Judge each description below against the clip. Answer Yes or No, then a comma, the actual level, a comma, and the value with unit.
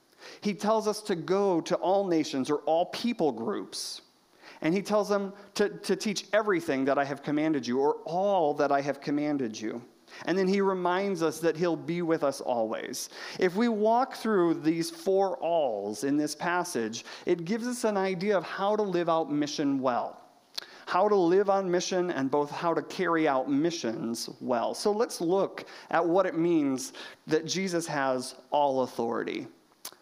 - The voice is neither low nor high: Yes, medium, 170 Hz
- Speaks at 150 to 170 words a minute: No, average, 180 wpm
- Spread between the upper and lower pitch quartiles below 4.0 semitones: No, average, 5.1 semitones